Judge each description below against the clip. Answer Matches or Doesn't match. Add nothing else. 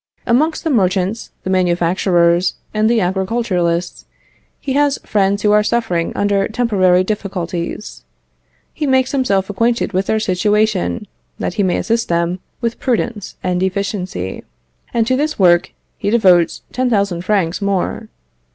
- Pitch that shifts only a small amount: Doesn't match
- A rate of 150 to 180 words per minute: Doesn't match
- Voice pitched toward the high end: Matches